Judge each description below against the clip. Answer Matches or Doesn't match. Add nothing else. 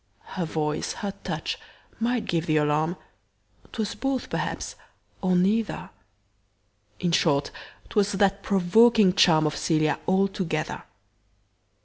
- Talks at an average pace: Doesn't match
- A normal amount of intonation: Matches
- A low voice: Doesn't match